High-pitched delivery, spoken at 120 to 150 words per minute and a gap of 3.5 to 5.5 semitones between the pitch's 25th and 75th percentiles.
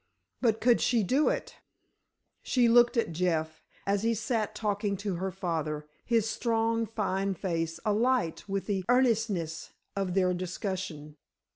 Yes: high, 200 Hz; average, 140 wpm; average, 4.2 semitones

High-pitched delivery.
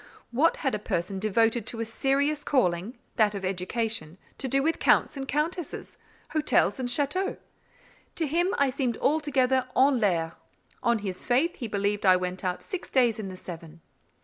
Yes: high, 235 Hz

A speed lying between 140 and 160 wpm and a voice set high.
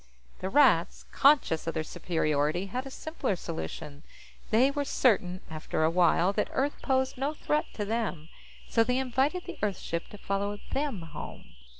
No: average, 170 wpm; high, 205 Hz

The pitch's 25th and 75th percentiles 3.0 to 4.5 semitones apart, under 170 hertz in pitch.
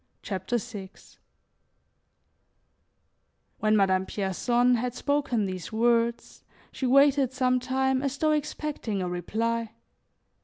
No: average, 4.1 semitones; high, 240 Hz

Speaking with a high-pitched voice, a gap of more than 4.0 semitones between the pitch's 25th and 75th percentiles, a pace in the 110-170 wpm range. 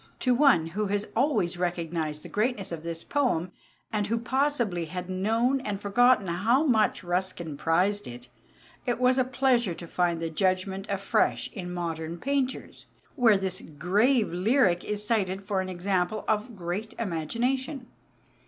Yes: high, 195 Hz; wide, 5.5 semitones; average, 155 wpm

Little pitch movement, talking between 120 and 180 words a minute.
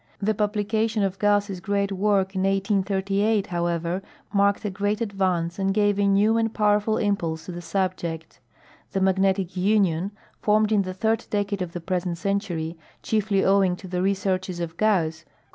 Yes: narrow, 2.2 semitones; average, 175 wpm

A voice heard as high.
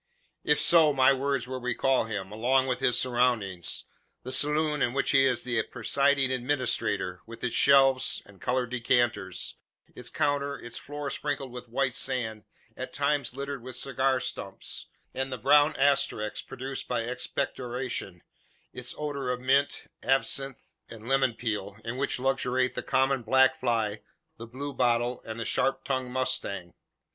No: low, 130 Hz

